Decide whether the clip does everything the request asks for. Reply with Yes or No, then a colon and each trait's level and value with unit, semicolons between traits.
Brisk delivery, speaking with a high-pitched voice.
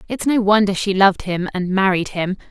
No: average, 190 wpm; high, 195 Hz